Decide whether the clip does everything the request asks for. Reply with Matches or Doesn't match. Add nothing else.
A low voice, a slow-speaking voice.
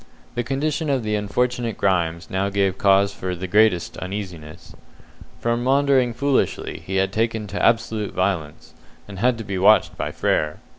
Doesn't match